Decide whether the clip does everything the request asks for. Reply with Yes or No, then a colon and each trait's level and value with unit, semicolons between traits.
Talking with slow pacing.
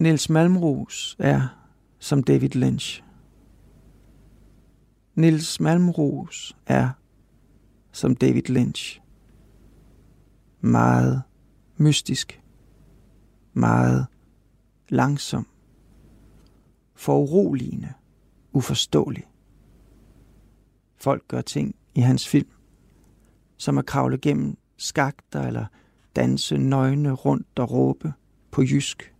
Yes: slow, 75 wpm